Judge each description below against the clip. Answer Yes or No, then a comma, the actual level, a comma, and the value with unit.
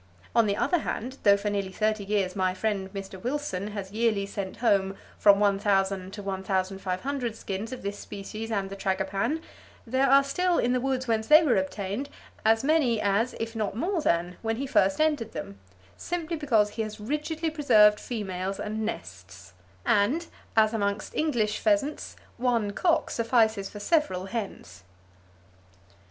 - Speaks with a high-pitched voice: Yes, high, 215 Hz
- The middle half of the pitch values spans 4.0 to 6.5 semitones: Yes, average, 4.6 semitones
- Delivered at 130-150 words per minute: No, average, 160 wpm